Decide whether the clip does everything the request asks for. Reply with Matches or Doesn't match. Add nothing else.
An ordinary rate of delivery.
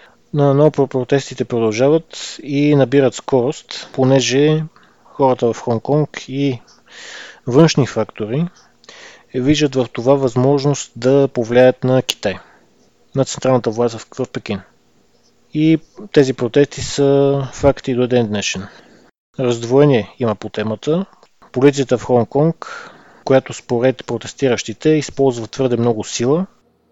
Doesn't match